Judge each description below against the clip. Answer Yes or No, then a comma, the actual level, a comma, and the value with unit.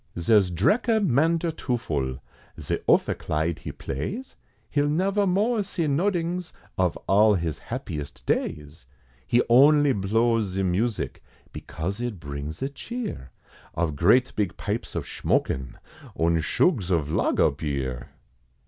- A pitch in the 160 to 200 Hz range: No, low, 105 Hz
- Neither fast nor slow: No, slow, 120 wpm